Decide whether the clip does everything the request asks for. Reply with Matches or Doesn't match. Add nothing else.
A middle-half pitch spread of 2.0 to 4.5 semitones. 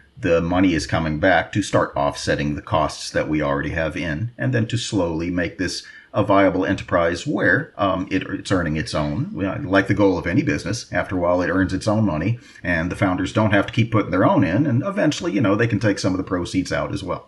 Matches